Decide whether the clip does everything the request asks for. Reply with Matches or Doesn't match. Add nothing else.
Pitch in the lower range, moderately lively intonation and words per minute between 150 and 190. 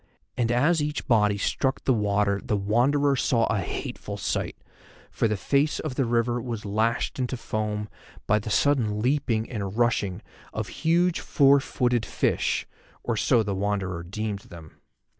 Matches